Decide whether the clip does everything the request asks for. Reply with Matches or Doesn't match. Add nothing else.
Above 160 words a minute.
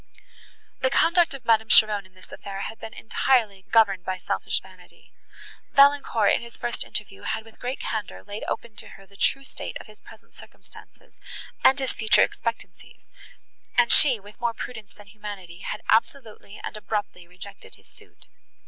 Matches